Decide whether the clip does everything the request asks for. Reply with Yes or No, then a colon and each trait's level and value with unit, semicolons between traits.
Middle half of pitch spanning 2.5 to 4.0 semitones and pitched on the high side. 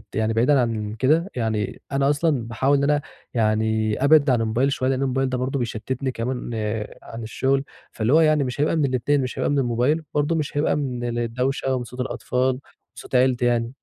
No: average, 3.2 semitones; low, 130 Hz